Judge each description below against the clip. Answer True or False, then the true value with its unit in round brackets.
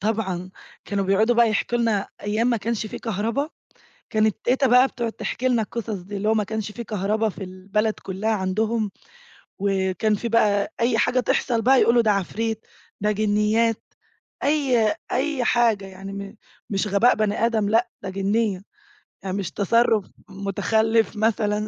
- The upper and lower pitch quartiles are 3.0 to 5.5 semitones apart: False (2.5 semitones)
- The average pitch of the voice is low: False (215 Hz)